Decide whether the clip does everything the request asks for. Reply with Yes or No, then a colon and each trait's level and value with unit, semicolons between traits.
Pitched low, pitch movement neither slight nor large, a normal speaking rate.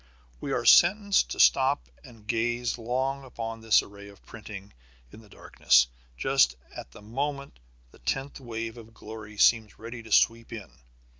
Yes: low, 115 Hz; average, 3.4 semitones; average, 160 wpm